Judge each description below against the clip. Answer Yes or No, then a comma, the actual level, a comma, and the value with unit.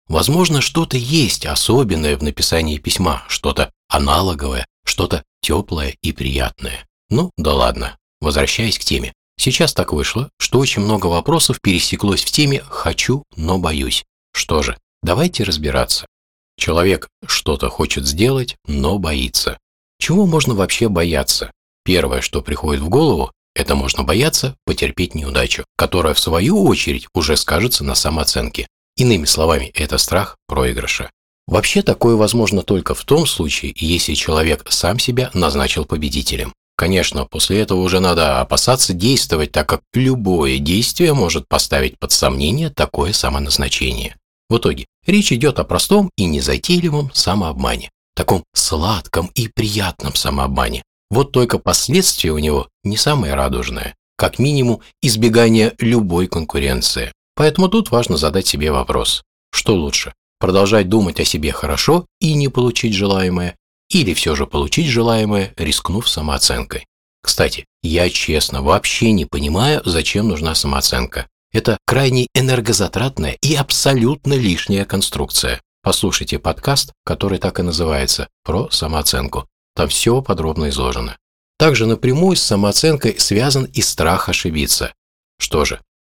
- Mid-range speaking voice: No, very low, 95 Hz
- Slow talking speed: No, average, 130 wpm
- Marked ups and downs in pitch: Yes, wide, 8.7 semitones